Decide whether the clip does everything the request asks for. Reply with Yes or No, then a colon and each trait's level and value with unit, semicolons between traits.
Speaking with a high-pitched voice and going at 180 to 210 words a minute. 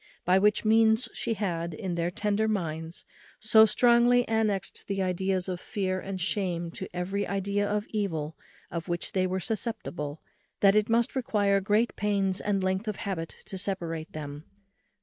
No: high, 195 Hz; average, 165 wpm